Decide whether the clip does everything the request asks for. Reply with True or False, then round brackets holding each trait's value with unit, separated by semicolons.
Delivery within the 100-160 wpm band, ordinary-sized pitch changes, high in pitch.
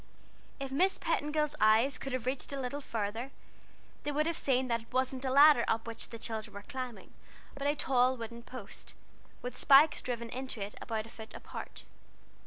False (190 wpm; 3.3 semitones; 255 Hz)